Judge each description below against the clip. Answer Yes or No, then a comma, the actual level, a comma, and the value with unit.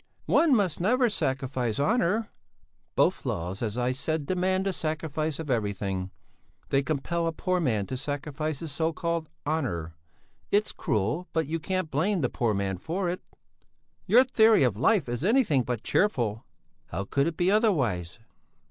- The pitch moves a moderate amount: No, wide, 7.1 semitones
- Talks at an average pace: Yes, average, 160 wpm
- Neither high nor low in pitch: Yes, medium, 155 Hz